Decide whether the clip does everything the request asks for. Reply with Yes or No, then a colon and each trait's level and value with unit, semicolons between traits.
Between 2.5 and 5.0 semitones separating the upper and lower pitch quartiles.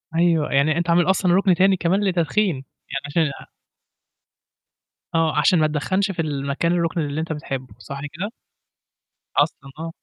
Yes: average, 3.4 semitones